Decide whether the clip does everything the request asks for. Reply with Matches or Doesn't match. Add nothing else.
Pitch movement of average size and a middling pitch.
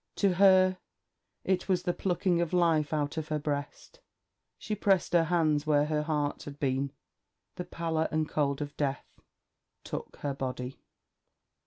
Matches